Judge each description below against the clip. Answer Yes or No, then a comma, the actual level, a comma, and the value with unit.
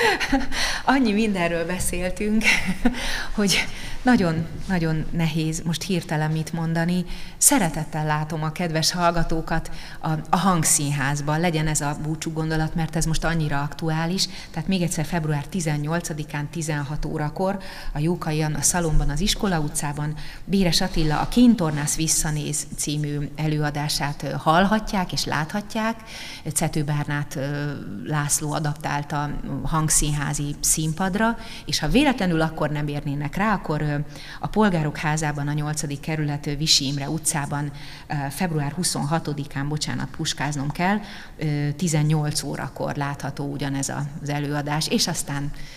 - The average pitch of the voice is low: No, medium, 155 Hz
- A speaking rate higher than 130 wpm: No, average, 115 wpm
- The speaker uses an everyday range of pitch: Yes, average, 3.1 semitones